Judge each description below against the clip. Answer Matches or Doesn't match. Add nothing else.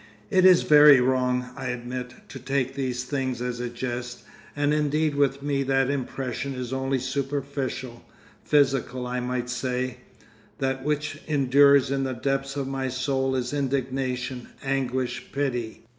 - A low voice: Matches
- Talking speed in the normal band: Matches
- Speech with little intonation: Matches